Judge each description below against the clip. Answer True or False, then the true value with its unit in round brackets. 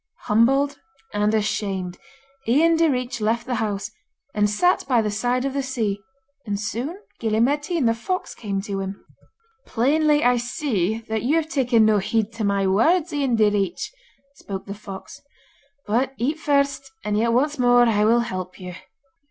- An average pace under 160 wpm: False (165 wpm)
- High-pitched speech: True (230 Hz)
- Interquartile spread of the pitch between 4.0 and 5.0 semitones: True (4.7 semitones)